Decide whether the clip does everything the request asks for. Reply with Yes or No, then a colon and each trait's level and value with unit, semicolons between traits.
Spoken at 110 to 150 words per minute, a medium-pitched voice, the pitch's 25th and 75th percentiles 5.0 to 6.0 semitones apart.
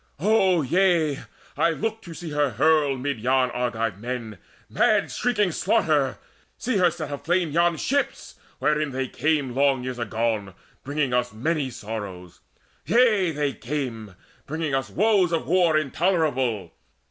Yes: average, 140 wpm; medium, 145 Hz; wide, 5.5 semitones